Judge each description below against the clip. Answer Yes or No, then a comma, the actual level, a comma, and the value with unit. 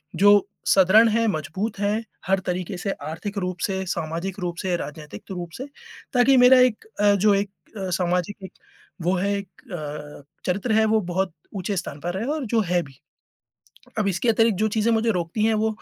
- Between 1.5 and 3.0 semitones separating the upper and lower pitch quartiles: No, average, 3.6 semitones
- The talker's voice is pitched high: Yes, high, 195 Hz